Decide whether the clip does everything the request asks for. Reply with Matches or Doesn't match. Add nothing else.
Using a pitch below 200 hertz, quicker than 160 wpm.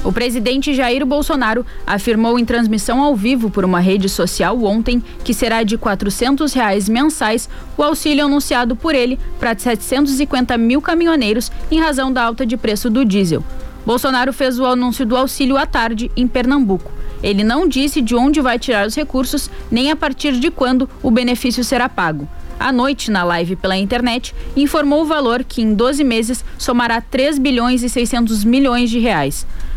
Doesn't match